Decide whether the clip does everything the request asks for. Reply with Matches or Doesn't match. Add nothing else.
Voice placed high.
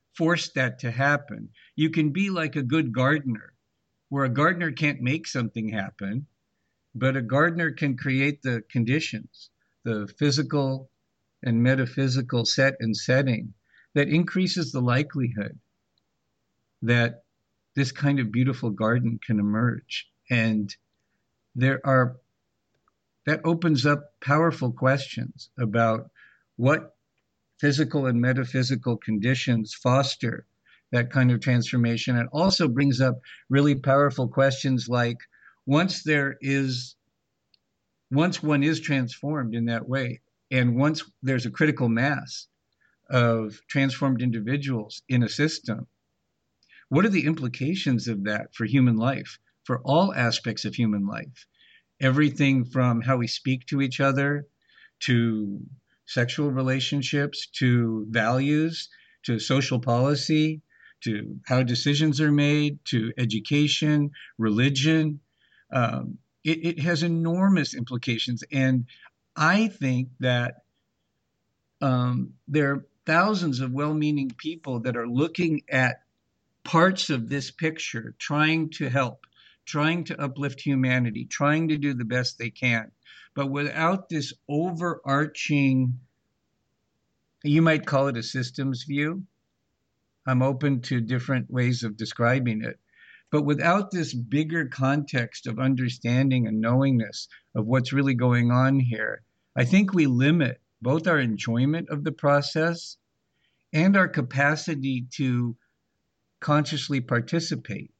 Doesn't match